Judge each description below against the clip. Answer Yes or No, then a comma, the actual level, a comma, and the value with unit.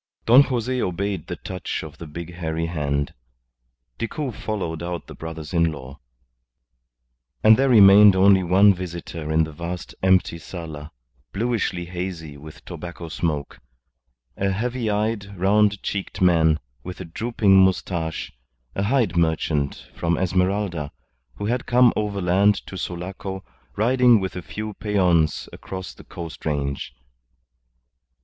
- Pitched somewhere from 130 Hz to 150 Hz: No, very low, 90 Hz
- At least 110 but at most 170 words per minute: Yes, slow, 135 wpm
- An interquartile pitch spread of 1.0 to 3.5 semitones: No, average, 3.9 semitones